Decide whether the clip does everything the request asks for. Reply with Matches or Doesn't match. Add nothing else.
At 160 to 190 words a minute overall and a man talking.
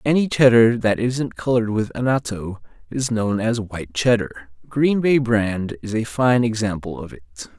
Matches